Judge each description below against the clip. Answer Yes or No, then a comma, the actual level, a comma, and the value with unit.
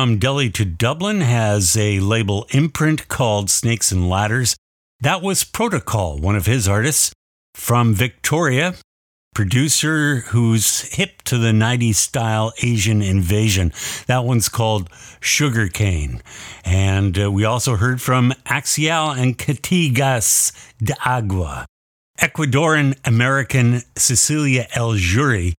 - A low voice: Yes, low, 115 Hz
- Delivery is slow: Yes, slow, 115 wpm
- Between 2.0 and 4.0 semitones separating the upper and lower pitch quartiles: No, average, 4.7 semitones